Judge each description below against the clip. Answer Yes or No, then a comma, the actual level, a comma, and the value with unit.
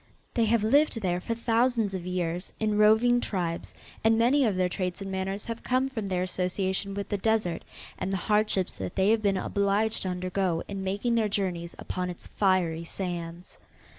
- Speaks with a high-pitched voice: Yes, high, 195 Hz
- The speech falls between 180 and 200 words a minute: Yes, average, 190 wpm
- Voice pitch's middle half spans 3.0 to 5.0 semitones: Yes, average, 3.3 semitones